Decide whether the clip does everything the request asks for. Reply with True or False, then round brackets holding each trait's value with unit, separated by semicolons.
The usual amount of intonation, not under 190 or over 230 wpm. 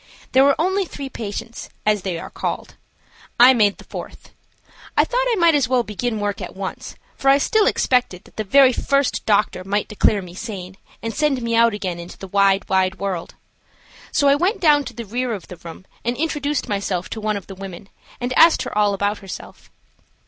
False (5.7 semitones; 205 wpm)